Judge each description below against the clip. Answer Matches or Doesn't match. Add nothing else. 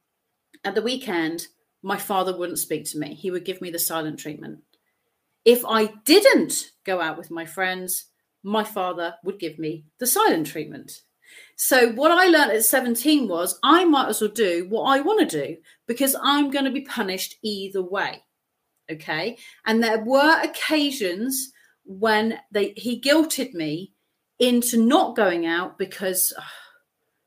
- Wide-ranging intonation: Matches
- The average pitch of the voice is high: Matches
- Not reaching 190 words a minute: Matches